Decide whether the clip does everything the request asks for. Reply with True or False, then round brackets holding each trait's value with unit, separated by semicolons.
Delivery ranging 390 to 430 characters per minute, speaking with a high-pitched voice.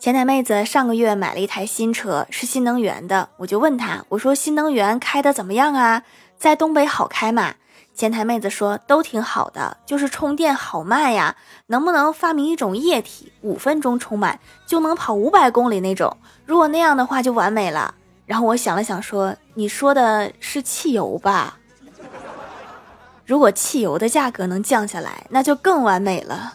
False (270 characters per minute; 245 Hz)